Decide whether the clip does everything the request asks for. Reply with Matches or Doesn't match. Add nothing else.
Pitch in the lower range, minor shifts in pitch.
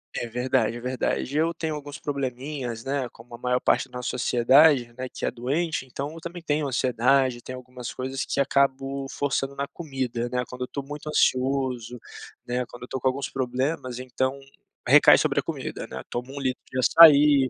Matches